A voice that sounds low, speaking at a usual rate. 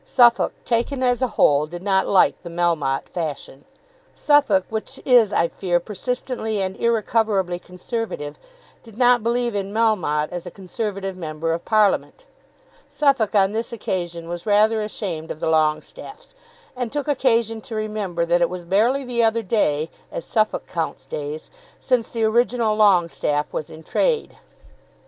No: high, 205 Hz; average, 155 wpm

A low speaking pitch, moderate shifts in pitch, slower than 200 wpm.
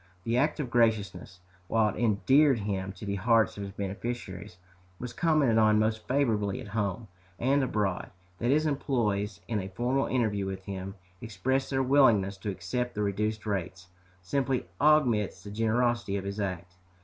Yes: low, 110 Hz; average, 3.9 semitones; average, 165 wpm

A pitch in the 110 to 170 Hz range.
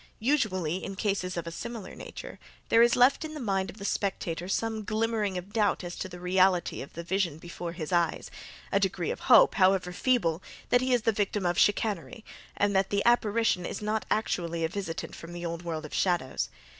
No: high, 190 Hz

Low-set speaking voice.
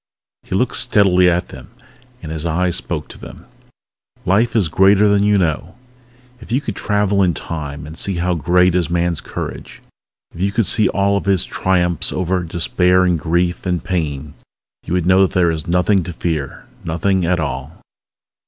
Yes: very low, 90 Hz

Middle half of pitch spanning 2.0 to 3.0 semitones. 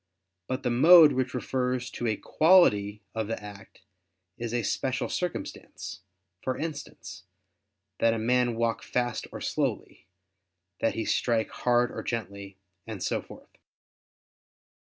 Yes: narrow, 2.6 semitones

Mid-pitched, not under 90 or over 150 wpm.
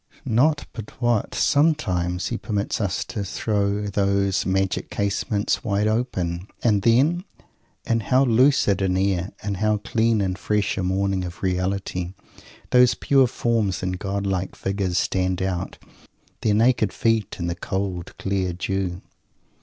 No: low, 100 Hz; average, 140 wpm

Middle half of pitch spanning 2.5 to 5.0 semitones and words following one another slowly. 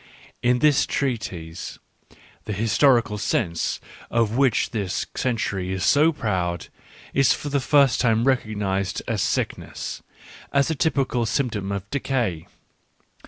No: wide, 5.6 semitones; slow, 130 wpm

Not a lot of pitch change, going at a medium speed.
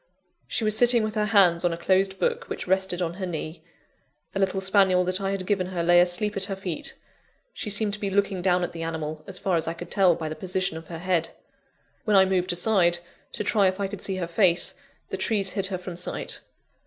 No: narrow, 2.1 semitones; fast, 240 wpm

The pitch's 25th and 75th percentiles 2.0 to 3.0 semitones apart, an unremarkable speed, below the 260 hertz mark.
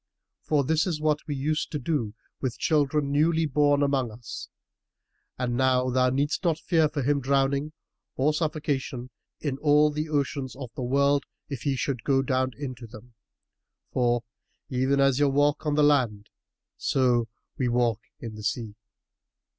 Yes: average, 2.7 semitones; average, 160 wpm; medium, 140 Hz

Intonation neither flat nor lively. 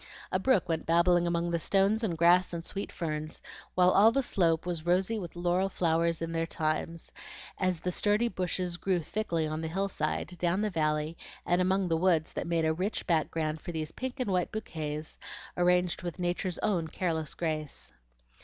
No: narrow, 2.3 semitones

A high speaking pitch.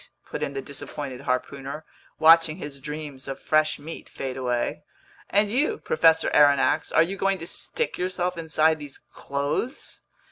No: medium, 155 Hz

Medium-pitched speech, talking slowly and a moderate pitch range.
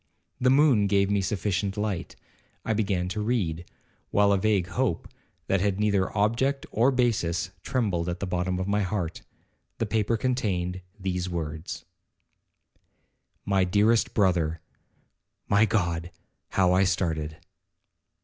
No: low, 100 Hz; slow, 130 wpm; average, 3.2 semitones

